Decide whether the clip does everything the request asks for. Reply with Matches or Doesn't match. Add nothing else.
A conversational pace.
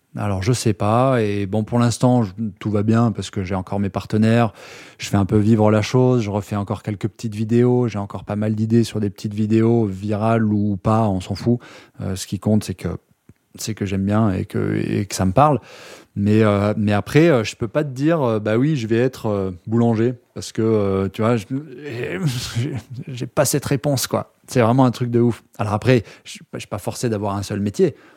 Doesn't match